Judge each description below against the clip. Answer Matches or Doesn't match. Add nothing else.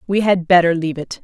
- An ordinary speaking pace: Doesn't match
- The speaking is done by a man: Doesn't match